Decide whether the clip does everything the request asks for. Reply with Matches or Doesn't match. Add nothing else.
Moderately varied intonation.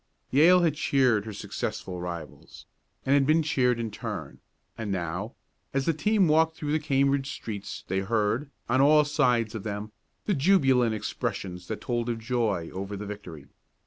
Doesn't match